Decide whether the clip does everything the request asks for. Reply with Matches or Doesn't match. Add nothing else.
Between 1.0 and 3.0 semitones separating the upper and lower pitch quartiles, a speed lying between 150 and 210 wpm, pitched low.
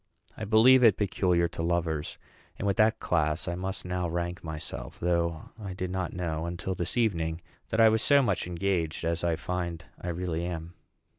Matches